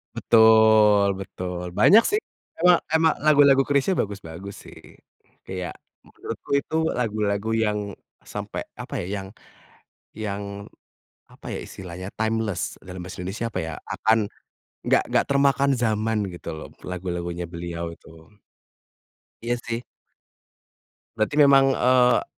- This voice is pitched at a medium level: No, low, 105 Hz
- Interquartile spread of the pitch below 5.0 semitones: No, wide, 5.4 semitones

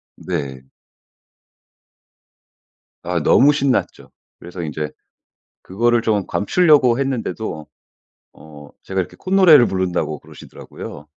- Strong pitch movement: Yes, wide, 8.9 semitones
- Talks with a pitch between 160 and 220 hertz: No, very low, 95 Hz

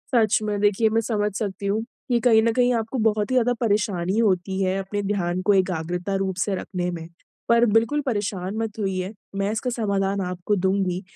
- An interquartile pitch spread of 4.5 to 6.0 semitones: No, average, 2.8 semitones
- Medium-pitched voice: No, high, 205 Hz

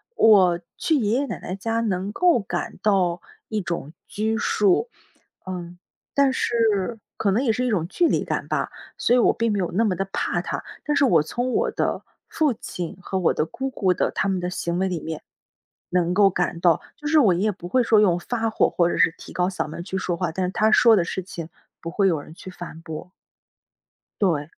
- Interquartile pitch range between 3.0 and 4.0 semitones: No, average, 4.5 semitones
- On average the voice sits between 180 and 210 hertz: Yes, high, 190 Hz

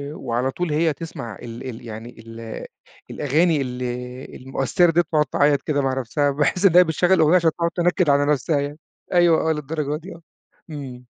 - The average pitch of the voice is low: No, medium, 145 Hz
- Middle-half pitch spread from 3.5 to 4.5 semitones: Yes, average, 4.0 semitones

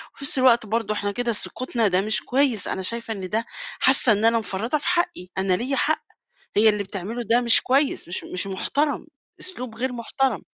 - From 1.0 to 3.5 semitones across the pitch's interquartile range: No, average, 4.1 semitones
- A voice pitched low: No, high, 230 Hz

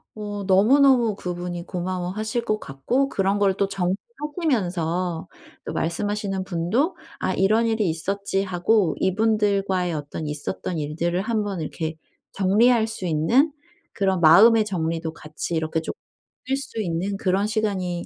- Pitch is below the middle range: No, high, 195 Hz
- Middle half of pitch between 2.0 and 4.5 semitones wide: Yes, average, 3.9 semitones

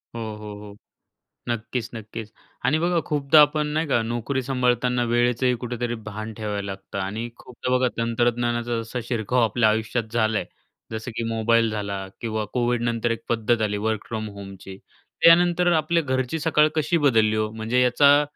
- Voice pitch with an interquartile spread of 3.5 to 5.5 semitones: No, narrow, 2.6 semitones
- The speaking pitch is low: Yes, low, 120 Hz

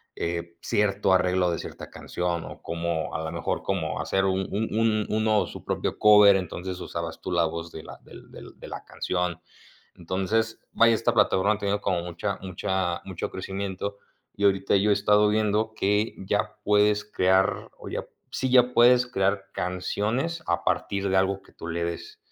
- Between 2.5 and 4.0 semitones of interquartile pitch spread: Yes, average, 2.8 semitones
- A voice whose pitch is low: Yes, very low, 95 Hz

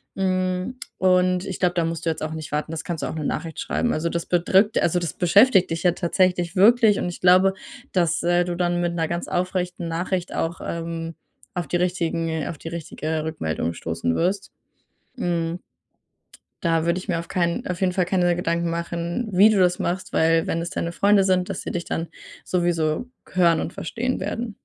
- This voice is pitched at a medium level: Yes, medium, 175 Hz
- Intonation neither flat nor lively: No, narrow, 1.8 semitones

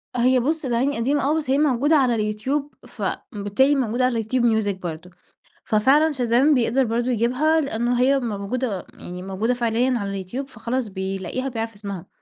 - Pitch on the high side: Yes, high, 240 Hz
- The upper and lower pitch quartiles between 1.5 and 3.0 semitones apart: No, average, 4.0 semitones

